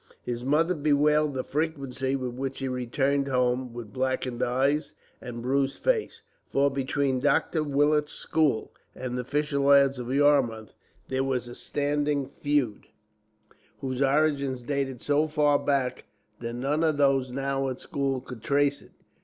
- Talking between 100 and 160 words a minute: Yes, average, 150 wpm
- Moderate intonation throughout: No, narrow, 2.2 semitones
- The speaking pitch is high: No, low, 135 Hz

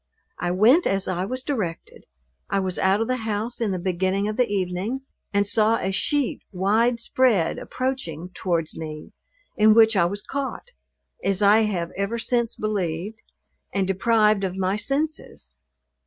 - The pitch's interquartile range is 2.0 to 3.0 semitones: No, average, 3.7 semitones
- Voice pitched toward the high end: Yes, high, 205 Hz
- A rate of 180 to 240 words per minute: No, average, 160 wpm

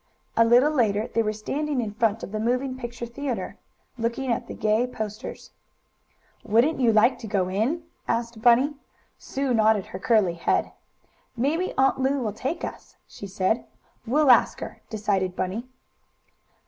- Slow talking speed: No, average, 160 wpm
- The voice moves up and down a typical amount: Yes, average, 3.5 semitones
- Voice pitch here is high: Yes, high, 230 Hz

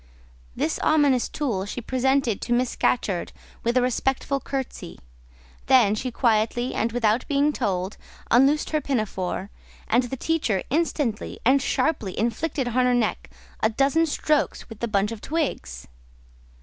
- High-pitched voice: Yes, high, 245 Hz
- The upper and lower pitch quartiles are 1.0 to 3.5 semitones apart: No, average, 4.3 semitones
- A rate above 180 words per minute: No, average, 145 wpm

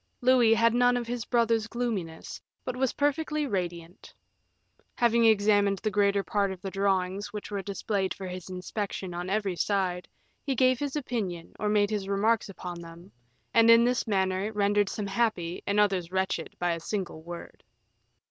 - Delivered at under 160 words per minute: No, average, 170 wpm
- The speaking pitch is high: Yes, high, 205 Hz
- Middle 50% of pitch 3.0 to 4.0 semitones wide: Yes, average, 3.7 semitones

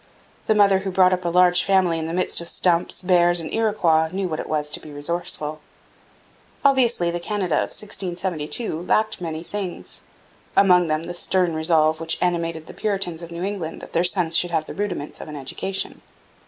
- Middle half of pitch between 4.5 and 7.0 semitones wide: No, average, 2.8 semitones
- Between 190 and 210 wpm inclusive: Yes, average, 195 wpm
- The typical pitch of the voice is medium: Yes, medium, 175 Hz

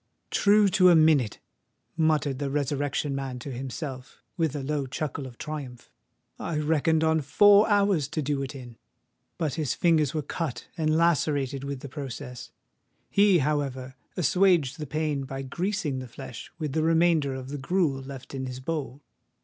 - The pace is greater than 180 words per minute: No, average, 165 wpm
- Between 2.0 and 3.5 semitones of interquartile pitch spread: Yes, average, 3.2 semitones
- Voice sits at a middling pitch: Yes, medium, 145 Hz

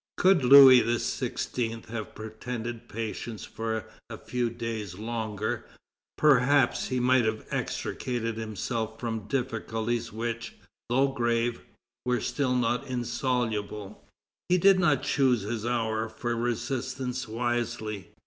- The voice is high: No, low, 120 Hz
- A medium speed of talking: No, slow, 115 wpm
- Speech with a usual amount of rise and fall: No, narrow, 2.1 semitones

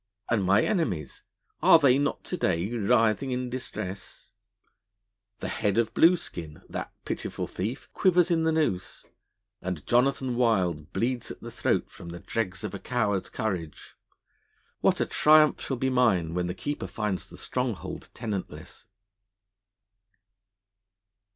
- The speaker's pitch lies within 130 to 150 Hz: No, low, 115 Hz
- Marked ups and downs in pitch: Yes, wide, 5.8 semitones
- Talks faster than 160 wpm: No, average, 140 wpm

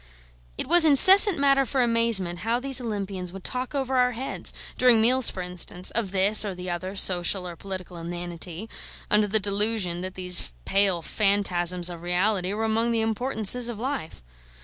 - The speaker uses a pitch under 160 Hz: No, high, 205 Hz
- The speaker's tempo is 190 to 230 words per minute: No, average, 170 wpm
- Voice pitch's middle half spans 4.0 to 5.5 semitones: Yes, average, 4.8 semitones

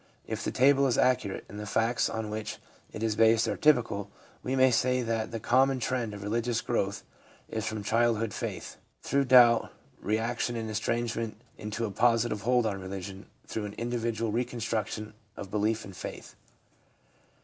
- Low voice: Yes, low, 115 Hz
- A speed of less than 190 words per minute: Yes, average, 165 wpm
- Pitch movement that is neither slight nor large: No, narrow, 2.3 semitones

